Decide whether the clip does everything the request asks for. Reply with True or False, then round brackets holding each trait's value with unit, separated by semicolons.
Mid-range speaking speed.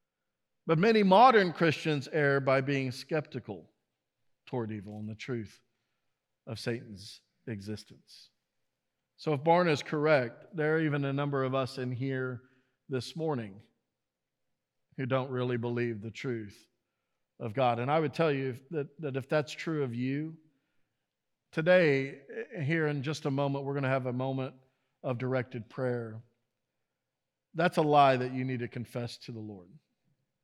True (155 wpm)